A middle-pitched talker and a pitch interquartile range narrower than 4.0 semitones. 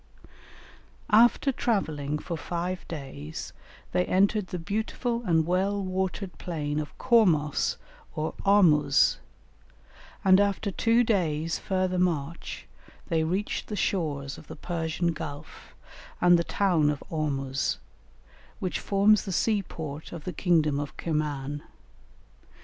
No: medium, 170 Hz; average, 4.5 semitones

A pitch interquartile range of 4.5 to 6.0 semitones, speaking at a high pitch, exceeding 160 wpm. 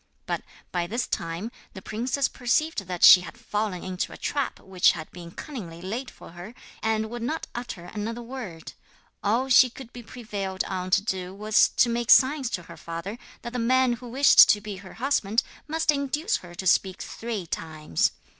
Yes: average, 5.3 semitones; high, 220 Hz; average, 190 wpm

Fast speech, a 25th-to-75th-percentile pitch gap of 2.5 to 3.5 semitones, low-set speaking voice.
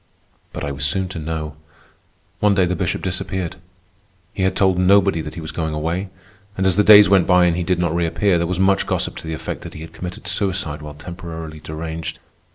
Yes: fast, 220 wpm; average, 2.9 semitones; very low, 90 Hz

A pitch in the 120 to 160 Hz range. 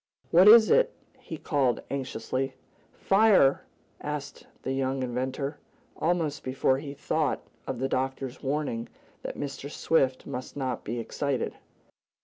Yes: low, 135 Hz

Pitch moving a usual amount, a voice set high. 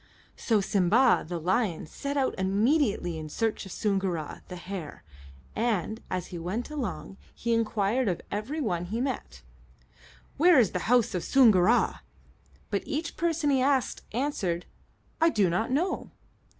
No: wide, 6.3 semitones; high, 215 Hz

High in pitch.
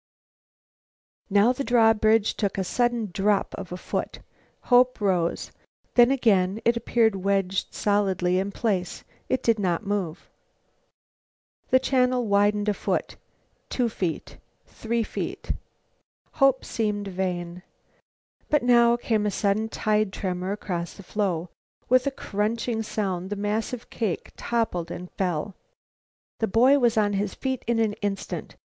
Yes: high, 210 Hz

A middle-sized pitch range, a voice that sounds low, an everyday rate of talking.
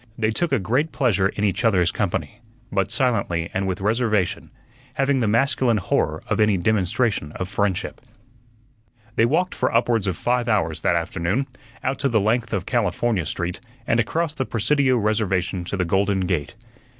Yes: average, 4.6 semitones; low, 105 Hz; average, 165 wpm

